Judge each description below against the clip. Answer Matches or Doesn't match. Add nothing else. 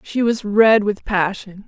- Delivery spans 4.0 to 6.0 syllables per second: Doesn't match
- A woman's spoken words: Matches